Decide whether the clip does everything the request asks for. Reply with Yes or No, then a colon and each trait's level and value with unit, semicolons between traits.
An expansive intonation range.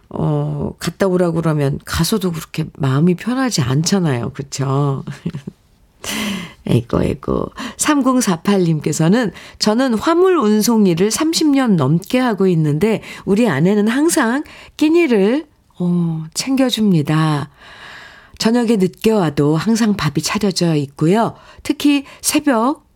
Yes: wide, 6.6 semitones